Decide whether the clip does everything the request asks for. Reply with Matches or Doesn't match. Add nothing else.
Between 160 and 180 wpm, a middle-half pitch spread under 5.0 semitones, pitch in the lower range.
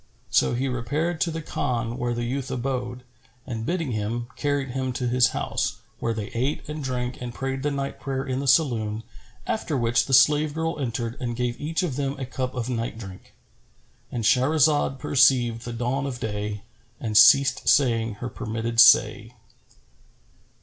Matches